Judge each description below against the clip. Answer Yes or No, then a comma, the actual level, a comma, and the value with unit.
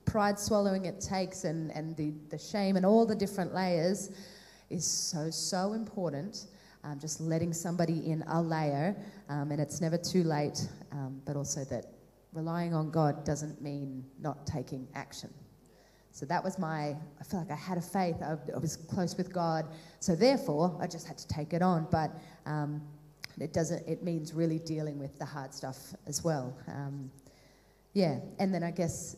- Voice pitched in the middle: Yes, medium, 160 Hz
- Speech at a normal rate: Yes, average, 185 wpm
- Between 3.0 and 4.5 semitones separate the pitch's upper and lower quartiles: Yes, average, 3.5 semitones